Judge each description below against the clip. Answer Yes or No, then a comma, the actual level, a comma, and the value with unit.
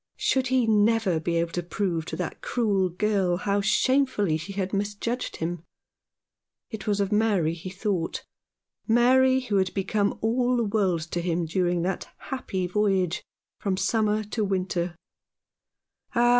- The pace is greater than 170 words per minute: No, average, 155 wpm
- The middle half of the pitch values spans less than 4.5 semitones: Yes, average, 3.8 semitones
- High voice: Yes, high, 200 Hz